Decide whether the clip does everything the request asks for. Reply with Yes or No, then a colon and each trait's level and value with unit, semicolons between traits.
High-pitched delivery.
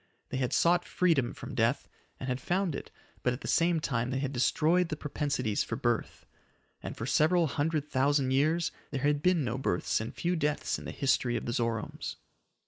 No: medium, 140 Hz